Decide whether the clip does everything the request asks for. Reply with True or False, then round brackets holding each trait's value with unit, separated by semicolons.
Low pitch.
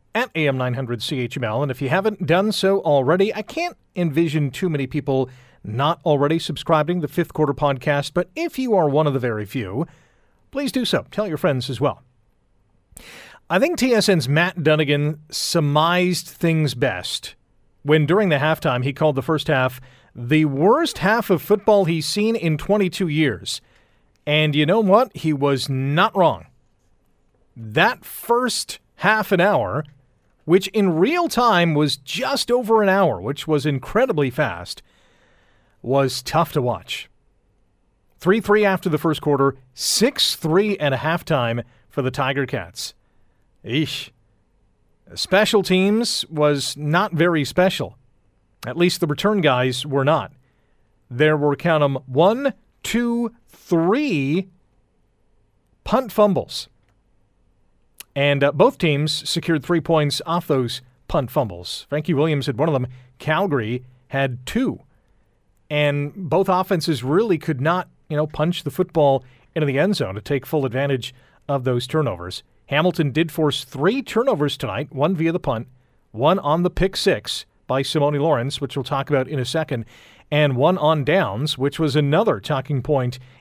False (150 Hz)